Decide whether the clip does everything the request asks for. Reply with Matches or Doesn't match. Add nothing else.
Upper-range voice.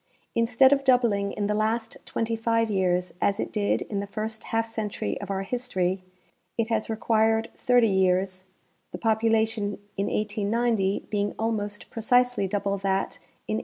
Matches